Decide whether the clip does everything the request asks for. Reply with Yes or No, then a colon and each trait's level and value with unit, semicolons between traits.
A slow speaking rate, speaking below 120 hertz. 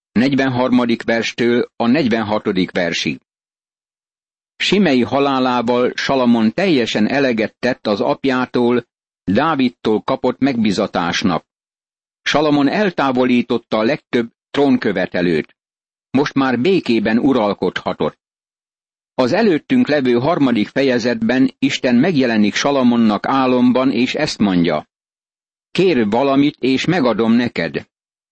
No: slow, 90 wpm; low, 125 Hz